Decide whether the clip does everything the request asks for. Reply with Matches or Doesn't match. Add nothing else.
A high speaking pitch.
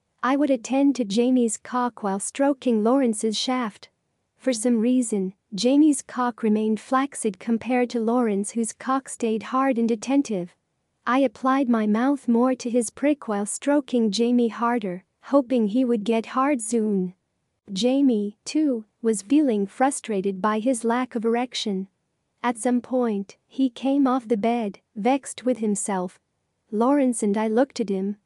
Matches